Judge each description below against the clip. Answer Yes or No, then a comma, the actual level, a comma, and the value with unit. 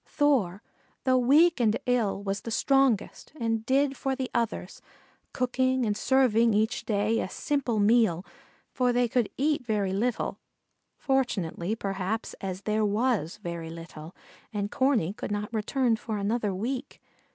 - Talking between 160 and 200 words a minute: No, average, 145 wpm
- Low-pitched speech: No, high, 225 Hz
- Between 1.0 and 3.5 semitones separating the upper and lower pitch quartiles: No, average, 4.2 semitones